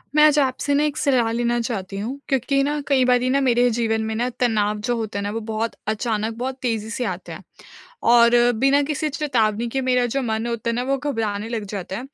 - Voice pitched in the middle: No, high, 240 Hz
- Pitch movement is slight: No, average, 3.4 semitones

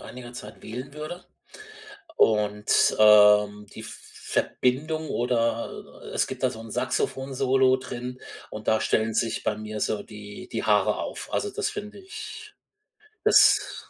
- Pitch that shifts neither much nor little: Yes, average, 4.0 semitones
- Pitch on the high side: No, low, 120 Hz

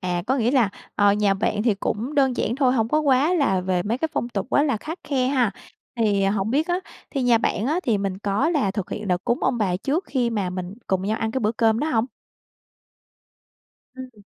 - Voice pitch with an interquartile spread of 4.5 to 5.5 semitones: Yes, average, 4.8 semitones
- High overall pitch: Yes, high, 225 Hz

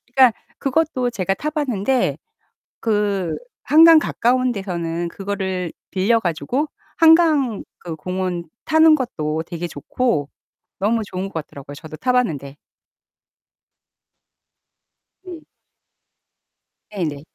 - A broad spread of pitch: Yes, wide, 7.1 semitones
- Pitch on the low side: No, high, 205 Hz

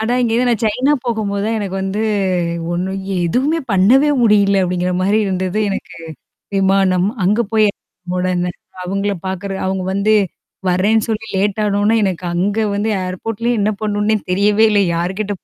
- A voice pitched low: No, high, 200 Hz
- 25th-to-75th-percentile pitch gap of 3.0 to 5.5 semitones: No, narrow, 2.5 semitones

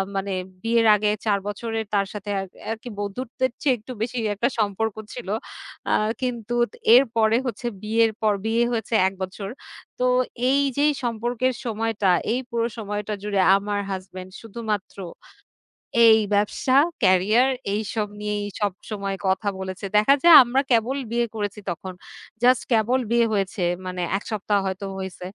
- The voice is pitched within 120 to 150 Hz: No, high, 215 Hz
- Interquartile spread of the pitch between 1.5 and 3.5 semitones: Yes, average, 2.9 semitones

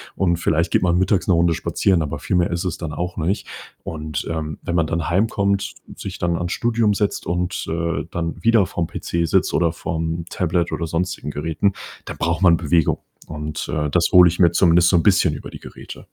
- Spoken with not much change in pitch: Yes, narrow, 1.8 semitones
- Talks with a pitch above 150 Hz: No, very low, 85 Hz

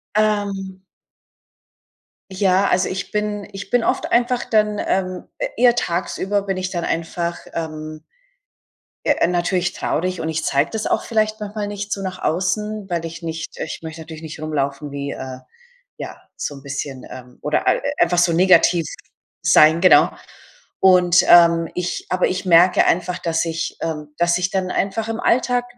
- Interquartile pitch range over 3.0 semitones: Yes, average, 3.6 semitones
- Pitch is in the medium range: Yes, medium, 180 Hz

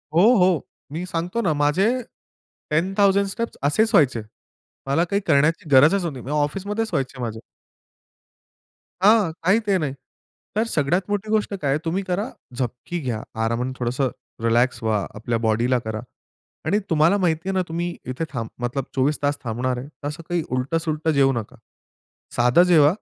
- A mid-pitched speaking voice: Yes, medium, 150 Hz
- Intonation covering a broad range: Yes, wide, 6.0 semitones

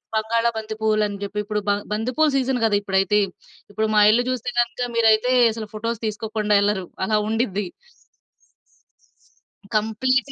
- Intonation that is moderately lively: No, narrow, 2.0 semitones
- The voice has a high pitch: Yes, high, 220 Hz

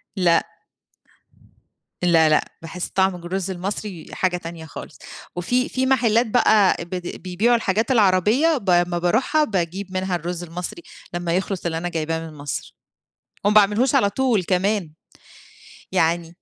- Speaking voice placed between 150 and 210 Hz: Yes, medium, 185 Hz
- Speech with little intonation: No, average, 3.7 semitones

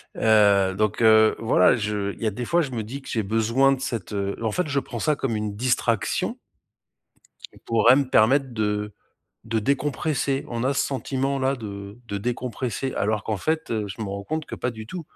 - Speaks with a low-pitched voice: Yes, low, 115 Hz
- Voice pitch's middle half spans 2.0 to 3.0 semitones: No, average, 4.2 semitones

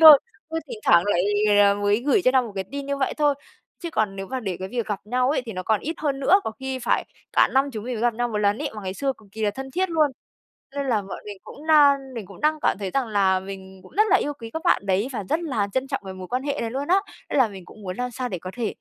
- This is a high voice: Yes, high, 245 Hz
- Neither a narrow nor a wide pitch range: No, wide, 5.7 semitones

